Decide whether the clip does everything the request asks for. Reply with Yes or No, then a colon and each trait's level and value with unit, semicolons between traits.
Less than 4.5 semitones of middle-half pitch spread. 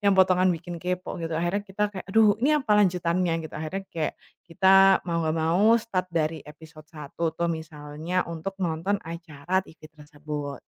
Yes: average, 3.1 semitones